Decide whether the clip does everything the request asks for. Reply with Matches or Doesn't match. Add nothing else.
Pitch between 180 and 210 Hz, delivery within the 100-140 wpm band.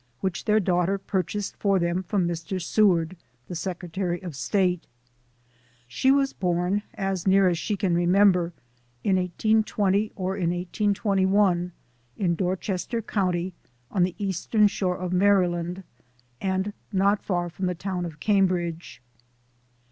Matches